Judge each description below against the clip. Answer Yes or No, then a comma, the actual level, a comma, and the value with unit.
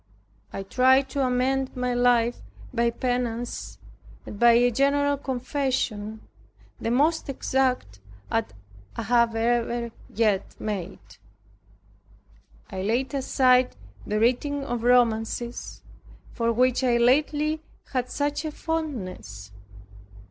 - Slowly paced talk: Yes, slow, 110 wpm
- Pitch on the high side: Yes, high, 245 Hz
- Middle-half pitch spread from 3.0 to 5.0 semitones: No, narrow, 2.6 semitones